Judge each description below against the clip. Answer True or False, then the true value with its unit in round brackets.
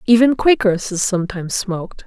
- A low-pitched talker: False (210 Hz)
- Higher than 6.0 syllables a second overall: True (6.3 syllables/s)